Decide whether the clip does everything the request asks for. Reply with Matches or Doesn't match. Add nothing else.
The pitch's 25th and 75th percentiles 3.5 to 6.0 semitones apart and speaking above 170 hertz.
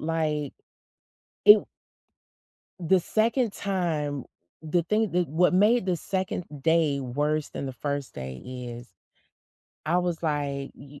Doesn't match